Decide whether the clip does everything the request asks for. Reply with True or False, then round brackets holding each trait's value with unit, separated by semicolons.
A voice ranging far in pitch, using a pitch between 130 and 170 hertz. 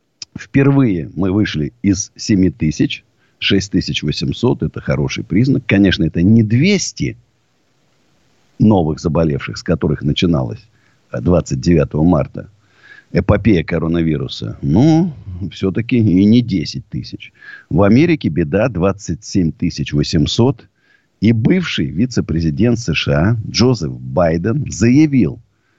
False (6.4 semitones; 100 Hz)